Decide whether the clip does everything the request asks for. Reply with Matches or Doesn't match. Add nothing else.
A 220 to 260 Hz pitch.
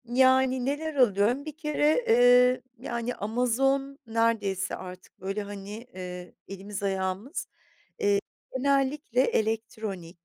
Matches